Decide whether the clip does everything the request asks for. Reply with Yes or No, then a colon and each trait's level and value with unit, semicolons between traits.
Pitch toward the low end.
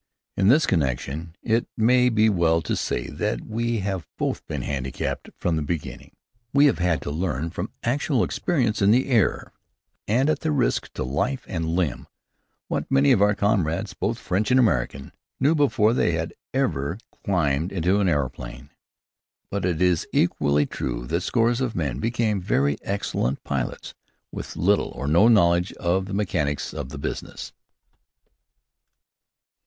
Yes: very low, 95 Hz